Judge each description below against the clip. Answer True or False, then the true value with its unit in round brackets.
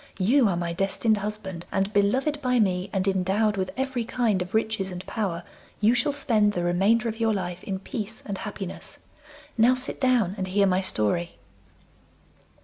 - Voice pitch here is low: False (205 Hz)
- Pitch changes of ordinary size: True (3.5 semitones)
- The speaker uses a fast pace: False (175 wpm)